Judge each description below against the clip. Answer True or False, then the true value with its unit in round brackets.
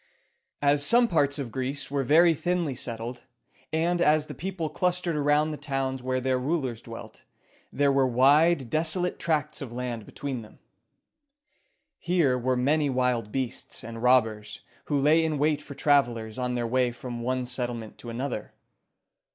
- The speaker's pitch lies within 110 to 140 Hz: True (135 Hz)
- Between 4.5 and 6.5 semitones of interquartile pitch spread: False (3.7 semitones)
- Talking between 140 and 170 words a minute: True (160 wpm)